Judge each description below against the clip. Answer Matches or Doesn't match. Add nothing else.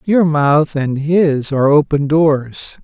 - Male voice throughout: Matches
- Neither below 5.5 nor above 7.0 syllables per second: Doesn't match